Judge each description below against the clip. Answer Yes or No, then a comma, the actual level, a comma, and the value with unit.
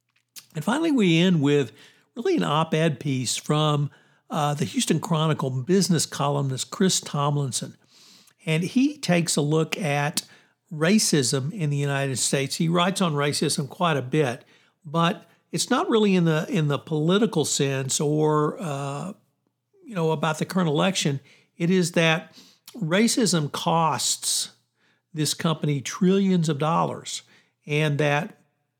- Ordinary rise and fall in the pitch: Yes, average, 3.5 semitones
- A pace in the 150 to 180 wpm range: No, average, 140 wpm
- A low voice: No, medium, 155 Hz